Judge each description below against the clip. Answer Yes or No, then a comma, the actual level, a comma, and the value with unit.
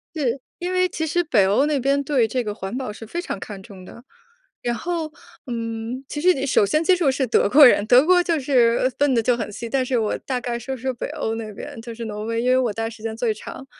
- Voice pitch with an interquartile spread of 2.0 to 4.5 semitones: Yes, average, 4.0 semitones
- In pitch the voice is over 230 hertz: Yes, high, 245 Hz